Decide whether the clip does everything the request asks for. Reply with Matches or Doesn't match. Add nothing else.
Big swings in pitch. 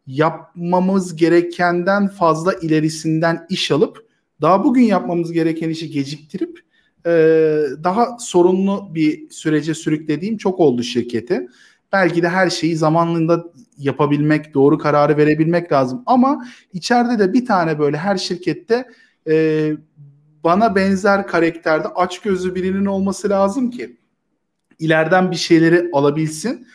Doesn't match